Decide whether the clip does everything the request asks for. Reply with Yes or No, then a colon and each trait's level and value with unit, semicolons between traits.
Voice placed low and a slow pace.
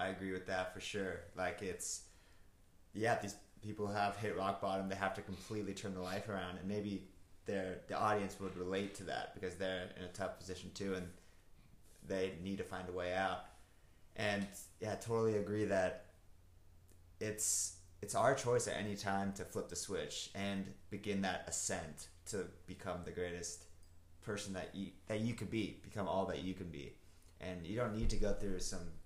No: very low, 95 Hz; average, 190 wpm